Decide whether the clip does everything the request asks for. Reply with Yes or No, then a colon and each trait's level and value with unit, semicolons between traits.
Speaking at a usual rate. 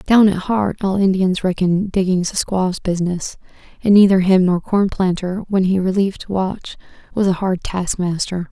Yes: average, 170 wpm